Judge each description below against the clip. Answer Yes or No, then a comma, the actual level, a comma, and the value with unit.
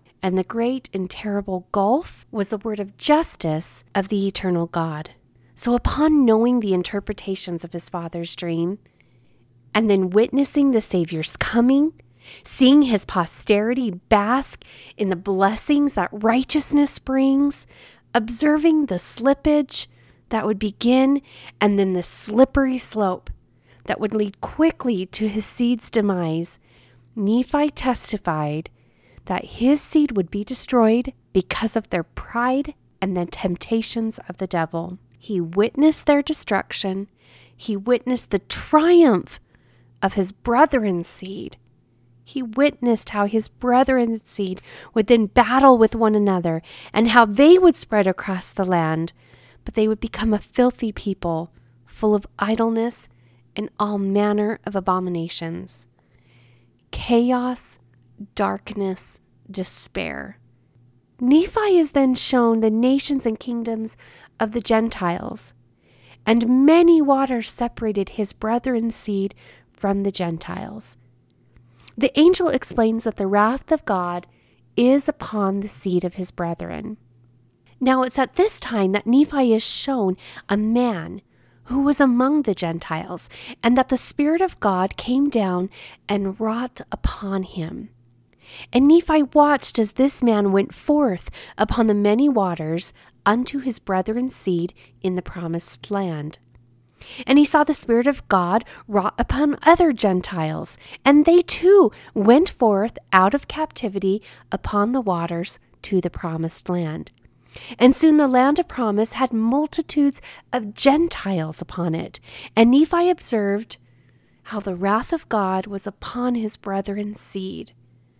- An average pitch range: No, wide, 6.2 semitones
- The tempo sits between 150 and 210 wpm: No, slow, 135 wpm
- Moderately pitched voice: No, high, 210 Hz